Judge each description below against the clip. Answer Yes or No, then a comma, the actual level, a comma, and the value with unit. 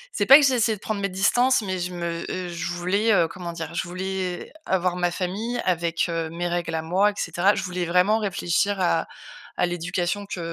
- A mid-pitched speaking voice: Yes, medium, 180 Hz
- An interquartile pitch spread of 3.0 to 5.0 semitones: No, narrow, 2.6 semitones